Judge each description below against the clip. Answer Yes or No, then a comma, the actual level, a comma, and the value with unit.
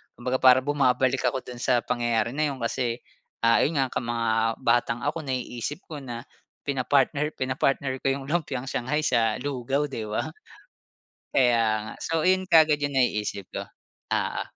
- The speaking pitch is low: Yes, low, 130 Hz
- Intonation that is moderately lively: Yes, average, 3.1 semitones